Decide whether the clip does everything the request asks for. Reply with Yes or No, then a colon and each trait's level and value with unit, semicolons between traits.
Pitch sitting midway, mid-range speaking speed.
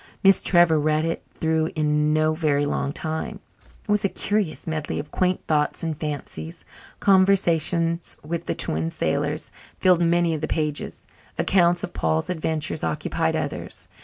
Yes: medium, 160 Hz; average, 155 wpm